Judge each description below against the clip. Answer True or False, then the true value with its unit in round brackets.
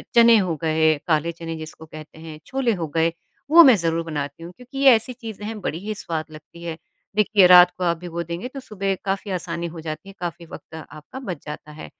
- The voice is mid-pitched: True (170 Hz)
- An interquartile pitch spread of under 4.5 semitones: False (4.9 semitones)